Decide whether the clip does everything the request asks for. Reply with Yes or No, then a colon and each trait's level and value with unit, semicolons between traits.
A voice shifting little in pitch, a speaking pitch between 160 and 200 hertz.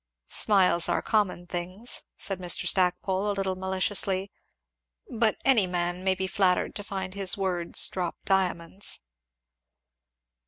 Yes: narrow, 1.7 semitones; high, 190 Hz